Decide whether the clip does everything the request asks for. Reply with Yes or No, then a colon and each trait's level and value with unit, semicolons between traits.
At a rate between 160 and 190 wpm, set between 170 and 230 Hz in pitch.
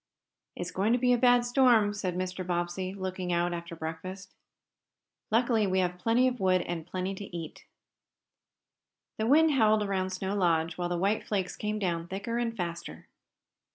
Yes: average, 170 wpm; high, 190 Hz